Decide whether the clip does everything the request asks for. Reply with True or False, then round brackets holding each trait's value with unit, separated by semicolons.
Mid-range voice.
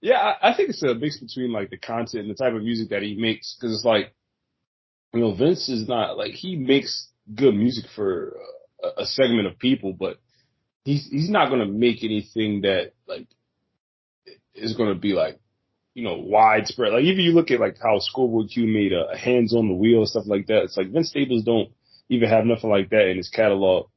False (115 Hz)